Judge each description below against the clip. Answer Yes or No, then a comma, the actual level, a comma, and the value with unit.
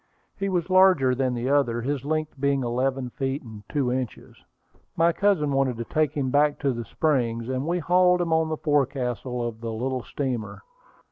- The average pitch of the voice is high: No, low, 135 Hz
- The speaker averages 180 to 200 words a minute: Yes, average, 190 wpm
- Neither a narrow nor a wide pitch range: Yes, average, 4.0 semitones